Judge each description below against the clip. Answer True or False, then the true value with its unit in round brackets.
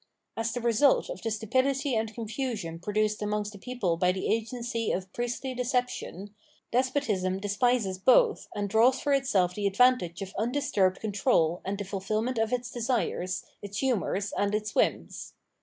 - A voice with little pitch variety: False (4.0 semitones)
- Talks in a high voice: True (220 Hz)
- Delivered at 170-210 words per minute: False (155 wpm)